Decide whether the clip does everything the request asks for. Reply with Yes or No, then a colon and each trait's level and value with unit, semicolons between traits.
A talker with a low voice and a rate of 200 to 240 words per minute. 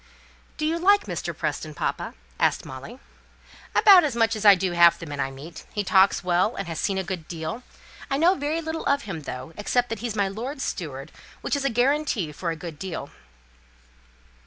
No: high, 200 Hz; fast, 205 wpm